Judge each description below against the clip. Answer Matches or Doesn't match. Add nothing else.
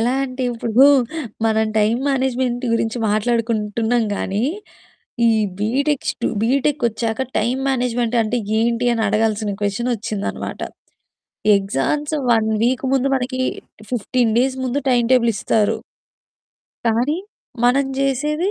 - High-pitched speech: Matches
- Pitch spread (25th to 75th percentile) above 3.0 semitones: Doesn't match